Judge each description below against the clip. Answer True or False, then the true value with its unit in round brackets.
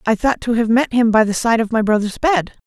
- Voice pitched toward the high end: True (230 Hz)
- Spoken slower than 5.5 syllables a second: False (5.6 syllables/s)